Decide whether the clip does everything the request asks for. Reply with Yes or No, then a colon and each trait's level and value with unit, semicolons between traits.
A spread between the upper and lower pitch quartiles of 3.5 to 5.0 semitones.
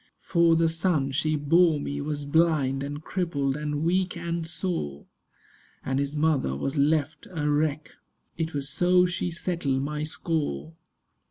No: average, 2.8 semitones